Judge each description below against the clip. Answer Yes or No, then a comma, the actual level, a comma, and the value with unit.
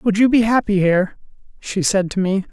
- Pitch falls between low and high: No, high, 200 Hz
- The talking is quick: Yes, fast, 215 wpm